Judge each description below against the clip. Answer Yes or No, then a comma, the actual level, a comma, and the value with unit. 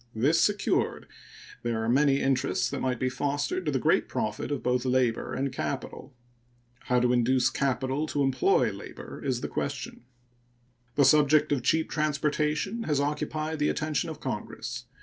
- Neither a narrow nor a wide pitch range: Yes, average, 3.0 semitones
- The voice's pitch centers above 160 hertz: No, medium, 140 Hz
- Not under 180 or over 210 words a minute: No, average, 160 wpm